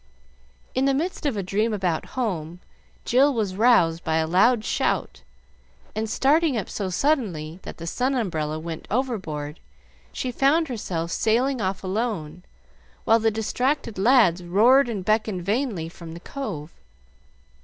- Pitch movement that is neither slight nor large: No, wide, 6.6 semitones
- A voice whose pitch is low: No, high, 215 Hz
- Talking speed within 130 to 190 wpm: Yes, average, 145 wpm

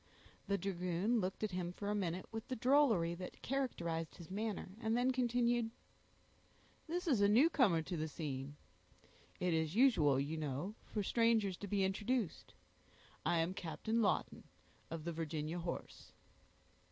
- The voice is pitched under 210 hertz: Yes, high, 190 Hz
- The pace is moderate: Yes, average, 155 wpm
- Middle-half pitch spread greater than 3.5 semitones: Yes, wide, 5.6 semitones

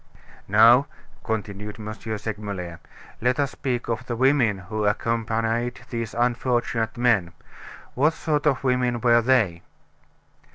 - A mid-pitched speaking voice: No, low, 115 Hz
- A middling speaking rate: No, slow, 120 wpm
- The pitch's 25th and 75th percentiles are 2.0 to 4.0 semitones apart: Yes, narrow, 2.5 semitones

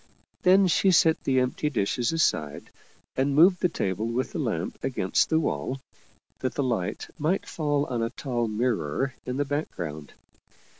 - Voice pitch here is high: No, low, 130 Hz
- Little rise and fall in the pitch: No, average, 5.1 semitones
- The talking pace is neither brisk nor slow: Yes, average, 160 wpm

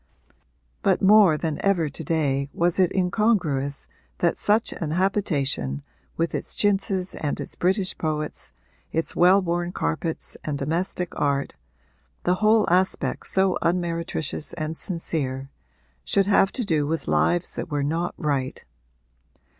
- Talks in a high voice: No, medium, 170 Hz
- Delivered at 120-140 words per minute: Yes, slow, 135 wpm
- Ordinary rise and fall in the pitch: Yes, average, 4.2 semitones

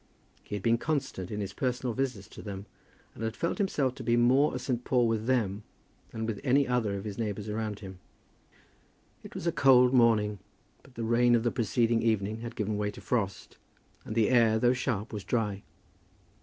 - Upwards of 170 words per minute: Yes, average, 200 wpm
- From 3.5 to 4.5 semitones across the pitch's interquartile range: No, average, 3.0 semitones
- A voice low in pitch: Yes, low, 115 Hz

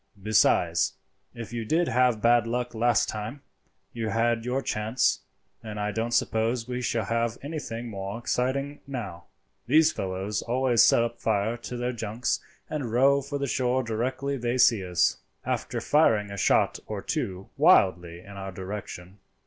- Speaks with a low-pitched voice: Yes, low, 115 Hz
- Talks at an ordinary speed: Yes, average, 155 wpm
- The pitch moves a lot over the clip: No, average, 3.2 semitones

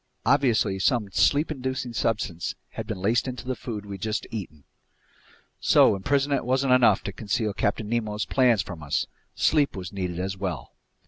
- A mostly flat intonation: No, average, 4.8 semitones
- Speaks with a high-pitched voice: No, low, 110 Hz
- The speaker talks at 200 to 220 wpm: No, average, 155 wpm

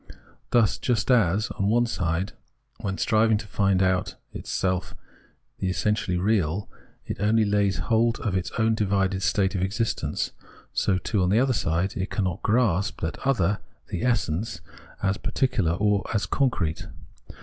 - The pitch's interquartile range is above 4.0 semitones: No, average, 3.0 semitones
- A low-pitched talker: Yes, low, 100 Hz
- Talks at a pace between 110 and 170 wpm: Yes, average, 150 wpm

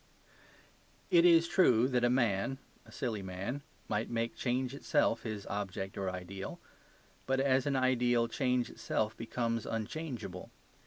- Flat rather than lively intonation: No, average, 4.0 semitones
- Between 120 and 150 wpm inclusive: Yes, average, 140 wpm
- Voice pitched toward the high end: No, low, 120 Hz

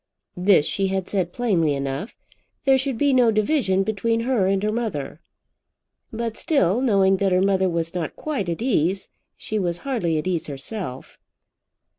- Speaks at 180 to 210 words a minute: No, average, 165 wpm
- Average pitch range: Yes, average, 4.9 semitones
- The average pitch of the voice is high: Yes, high, 195 Hz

